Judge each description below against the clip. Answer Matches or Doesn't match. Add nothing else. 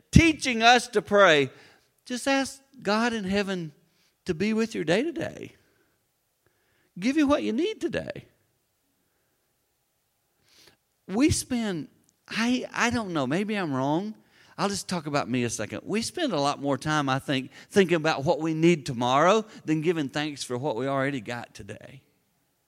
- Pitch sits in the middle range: Matches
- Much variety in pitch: Matches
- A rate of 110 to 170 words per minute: Matches